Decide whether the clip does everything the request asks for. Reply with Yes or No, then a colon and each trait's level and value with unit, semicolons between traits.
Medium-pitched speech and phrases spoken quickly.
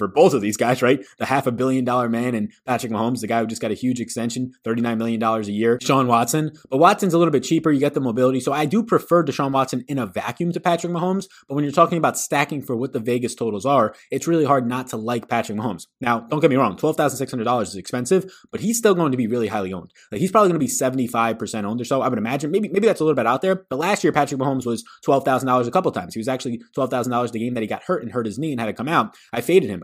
No: low, 130 Hz; fast, 300 wpm